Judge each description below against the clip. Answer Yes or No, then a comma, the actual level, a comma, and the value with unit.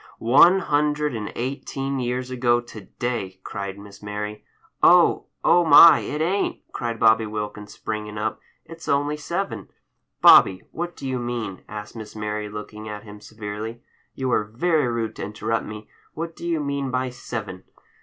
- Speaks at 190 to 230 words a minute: No, average, 165 wpm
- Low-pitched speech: Yes, low, 115 Hz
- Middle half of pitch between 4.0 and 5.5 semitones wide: Yes, average, 4.9 semitones